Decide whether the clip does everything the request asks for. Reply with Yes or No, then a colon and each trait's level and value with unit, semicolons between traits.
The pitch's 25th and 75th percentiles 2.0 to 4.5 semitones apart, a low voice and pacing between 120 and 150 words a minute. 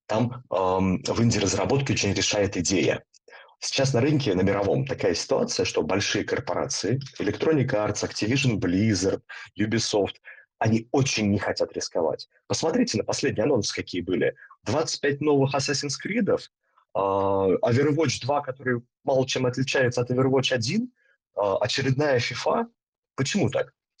No: average, 5.2 semitones; low, 125 Hz; average, 130 wpm